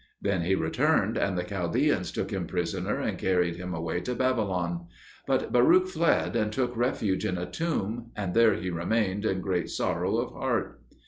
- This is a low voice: Yes, very low, 95 Hz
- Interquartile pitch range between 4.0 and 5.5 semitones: Yes, average, 4.9 semitones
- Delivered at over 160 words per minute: Yes, average, 180 wpm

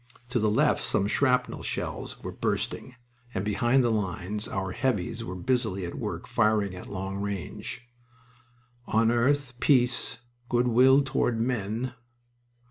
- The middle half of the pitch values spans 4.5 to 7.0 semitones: No, average, 4.0 semitones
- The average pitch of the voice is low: Yes, low, 115 Hz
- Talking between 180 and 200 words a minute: No, slow, 135 wpm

